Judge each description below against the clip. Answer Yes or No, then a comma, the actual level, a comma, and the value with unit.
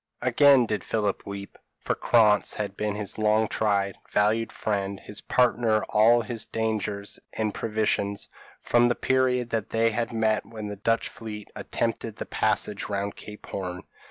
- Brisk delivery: No, average, 165 wpm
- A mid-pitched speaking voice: No, low, 110 Hz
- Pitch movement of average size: No, narrow, 1.9 semitones